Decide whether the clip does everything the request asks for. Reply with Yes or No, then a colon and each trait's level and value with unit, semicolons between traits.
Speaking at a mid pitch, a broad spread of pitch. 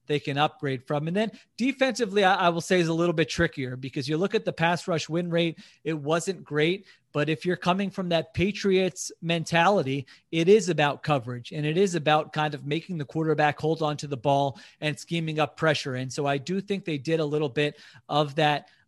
No: medium, 160 Hz; average, 3.2 semitones